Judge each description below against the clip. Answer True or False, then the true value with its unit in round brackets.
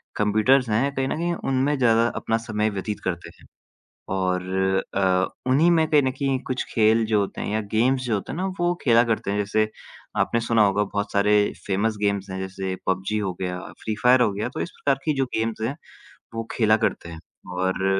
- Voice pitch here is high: False (110 Hz)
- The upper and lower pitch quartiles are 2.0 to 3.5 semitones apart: False (4.5 semitones)